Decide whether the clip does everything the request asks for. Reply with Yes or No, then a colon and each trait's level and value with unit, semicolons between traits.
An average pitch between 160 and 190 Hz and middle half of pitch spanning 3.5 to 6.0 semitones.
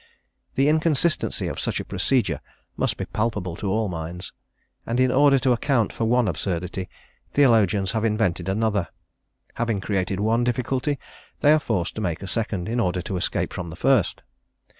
No: low, 110 Hz; average, 5.1 semitones